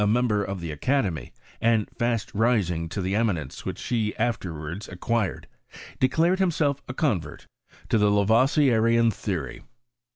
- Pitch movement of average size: Yes, average, 4.5 semitones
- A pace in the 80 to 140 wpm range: Yes, slow, 135 wpm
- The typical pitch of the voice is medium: No, low, 110 Hz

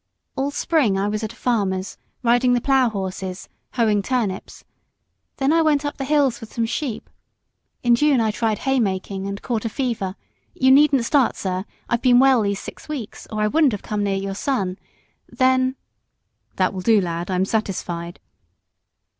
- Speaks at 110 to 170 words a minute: No, average, 180 wpm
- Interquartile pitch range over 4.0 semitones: Yes, average, 5.0 semitones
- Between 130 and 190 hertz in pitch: No, high, 225 Hz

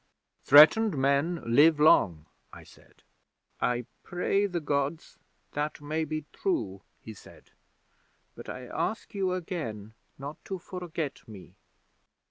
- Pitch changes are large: Yes, wide, 5.7 semitones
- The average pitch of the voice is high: No, medium, 150 Hz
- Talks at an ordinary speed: No, slow, 120 wpm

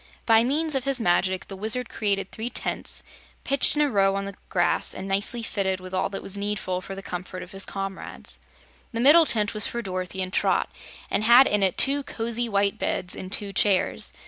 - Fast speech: Yes, fast, 210 wpm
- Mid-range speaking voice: No, high, 200 Hz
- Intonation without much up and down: No, average, 3.8 semitones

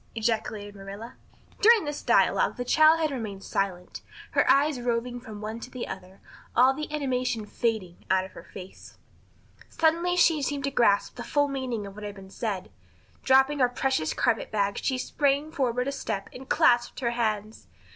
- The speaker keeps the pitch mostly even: No, average, 5.1 semitones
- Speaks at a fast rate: No, average, 175 wpm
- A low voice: No, high, 245 Hz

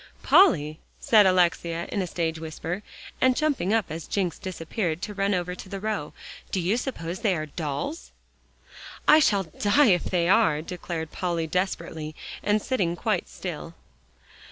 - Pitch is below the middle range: No, medium, 180 Hz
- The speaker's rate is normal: Yes, average, 155 wpm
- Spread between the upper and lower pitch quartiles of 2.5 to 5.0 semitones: Yes, average, 4.1 semitones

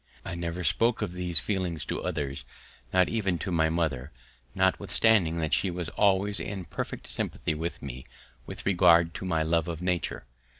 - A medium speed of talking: Yes, average, 170 wpm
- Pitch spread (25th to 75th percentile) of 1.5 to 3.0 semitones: Yes, average, 2.7 semitones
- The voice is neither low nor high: No, very low, 85 Hz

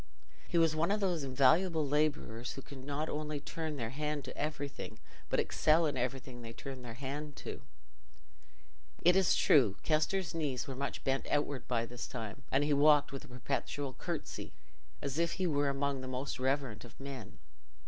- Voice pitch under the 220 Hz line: Yes, medium, 140 Hz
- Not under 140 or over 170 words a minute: No, average, 180 wpm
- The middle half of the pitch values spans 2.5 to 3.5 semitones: Yes, average, 2.9 semitones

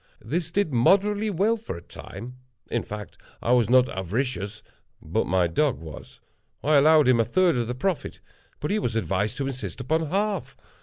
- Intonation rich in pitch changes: Yes, wide, 7.0 semitones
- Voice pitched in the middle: No, low, 130 Hz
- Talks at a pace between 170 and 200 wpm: Yes, average, 175 wpm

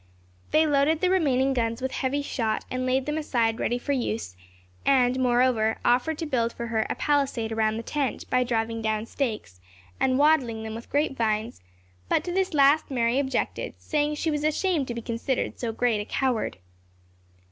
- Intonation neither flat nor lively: Yes, average, 4.0 semitones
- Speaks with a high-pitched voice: Yes, very high, 255 Hz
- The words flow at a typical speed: Yes, average, 185 wpm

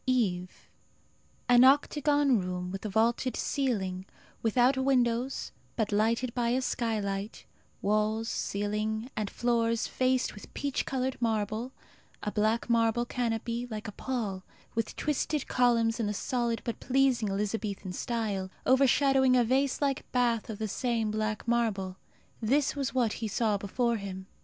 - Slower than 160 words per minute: Yes, average, 140 wpm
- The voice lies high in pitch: Yes, high, 230 Hz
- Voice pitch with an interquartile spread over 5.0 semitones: No, average, 3.1 semitones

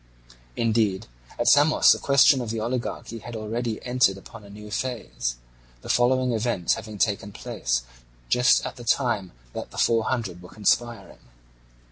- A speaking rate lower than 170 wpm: Yes, average, 155 wpm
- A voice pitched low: Yes, low, 115 Hz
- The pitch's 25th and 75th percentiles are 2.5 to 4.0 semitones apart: Yes, average, 3.1 semitones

